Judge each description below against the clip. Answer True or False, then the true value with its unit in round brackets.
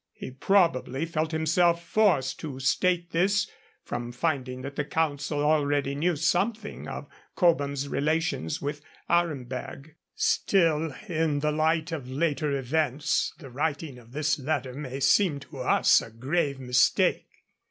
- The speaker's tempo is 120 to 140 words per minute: True (135 wpm)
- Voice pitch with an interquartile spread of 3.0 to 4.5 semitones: True (3.5 semitones)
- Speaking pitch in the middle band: True (150 Hz)